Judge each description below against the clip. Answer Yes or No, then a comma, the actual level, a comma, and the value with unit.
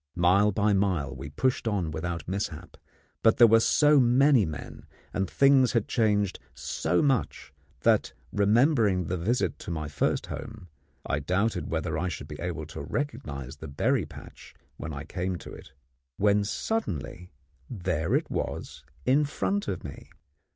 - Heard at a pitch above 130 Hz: No, very low, 95 Hz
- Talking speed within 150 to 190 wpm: Yes, average, 160 wpm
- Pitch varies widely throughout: Yes, wide, 6.0 semitones